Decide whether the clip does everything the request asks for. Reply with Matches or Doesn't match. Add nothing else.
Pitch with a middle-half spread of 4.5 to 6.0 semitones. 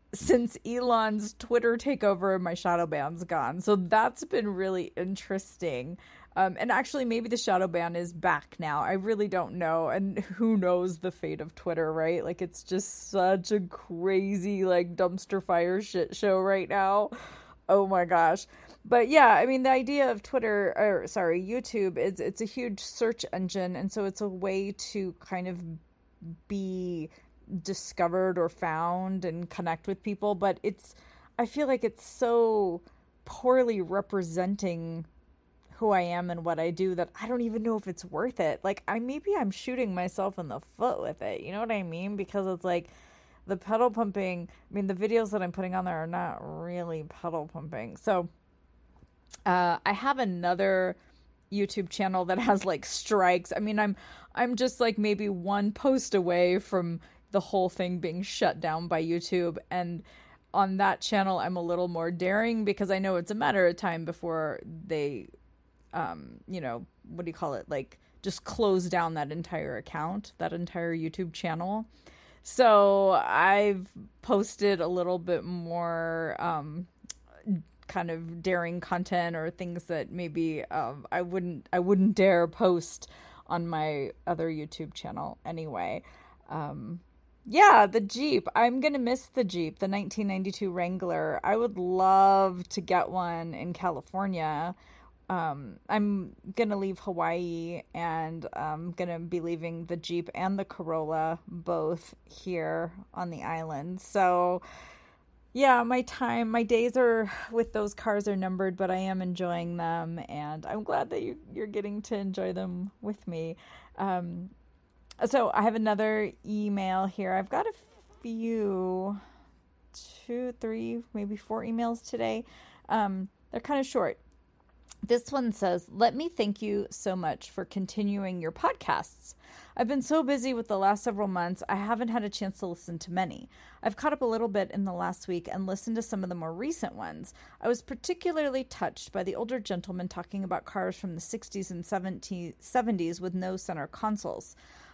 Doesn't match